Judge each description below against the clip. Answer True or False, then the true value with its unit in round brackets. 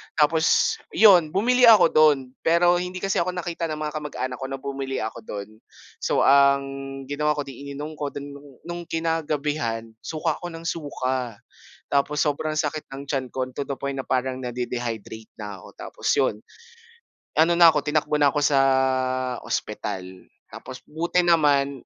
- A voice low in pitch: False (145 Hz)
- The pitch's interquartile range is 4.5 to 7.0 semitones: False (3.6 semitones)